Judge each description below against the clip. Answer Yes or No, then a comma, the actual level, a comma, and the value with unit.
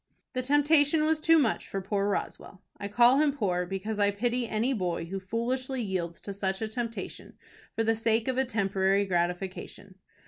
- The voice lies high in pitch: Yes, high, 220 Hz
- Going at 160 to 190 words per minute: Yes, average, 180 wpm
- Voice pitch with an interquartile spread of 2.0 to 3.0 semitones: No, average, 4.8 semitones